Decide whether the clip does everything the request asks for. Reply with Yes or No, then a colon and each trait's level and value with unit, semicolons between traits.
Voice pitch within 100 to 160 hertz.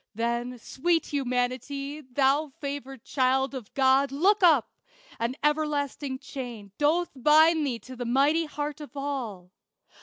No: very high, 275 Hz